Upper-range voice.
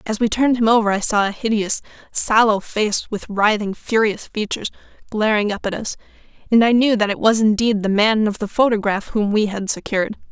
Yes: high, 215 Hz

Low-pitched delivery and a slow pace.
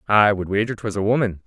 No: low, 105 Hz; fast, 245 wpm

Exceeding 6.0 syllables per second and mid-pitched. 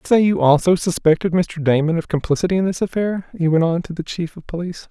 Yes: 6.3 syllables/s; medium, 170 Hz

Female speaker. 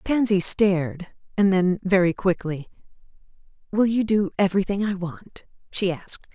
Yes: female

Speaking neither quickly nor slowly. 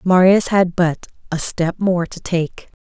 Yes: average, 170 wpm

